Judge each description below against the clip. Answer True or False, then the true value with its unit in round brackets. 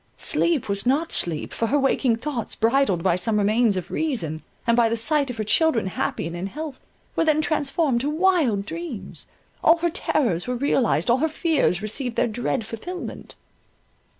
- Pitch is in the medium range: False (245 Hz)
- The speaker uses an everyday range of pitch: False (6.2 semitones)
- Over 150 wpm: True (180 wpm)